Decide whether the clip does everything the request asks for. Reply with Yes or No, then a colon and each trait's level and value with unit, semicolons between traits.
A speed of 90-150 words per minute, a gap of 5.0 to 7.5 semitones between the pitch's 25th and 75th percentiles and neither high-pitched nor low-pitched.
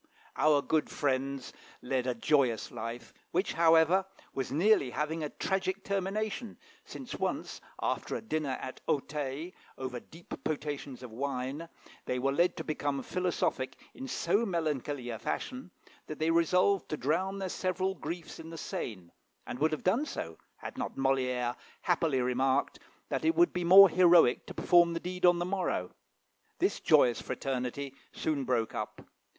No: average, 160 wpm; wide, 5.5 semitones; medium, 155 Hz